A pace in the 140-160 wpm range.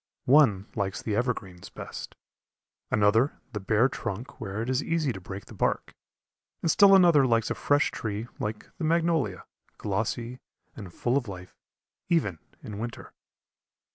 Yes: average, 150 wpm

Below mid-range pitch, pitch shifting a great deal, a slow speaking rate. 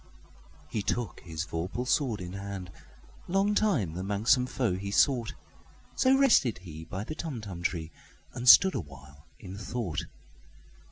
Yes: low, 100 Hz; wide, 6.3 semitones; slow, 125 wpm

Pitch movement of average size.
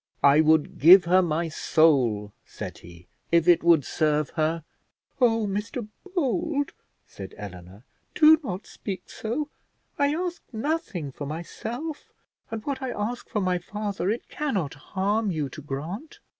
No: wide, 7.9 semitones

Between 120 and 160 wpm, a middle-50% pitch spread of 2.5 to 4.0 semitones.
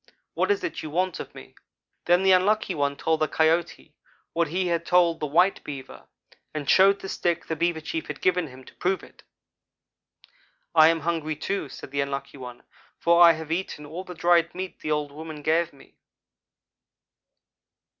No: average, 185 wpm; average, 3.0 semitones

